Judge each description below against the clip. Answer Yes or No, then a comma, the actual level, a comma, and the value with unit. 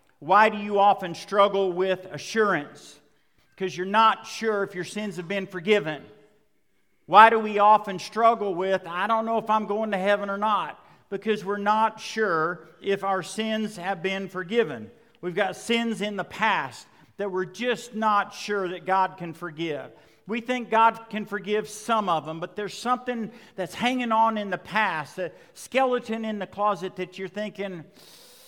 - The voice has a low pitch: No, high, 205 Hz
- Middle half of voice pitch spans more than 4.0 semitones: No, average, 2.8 semitones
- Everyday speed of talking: Yes, average, 175 wpm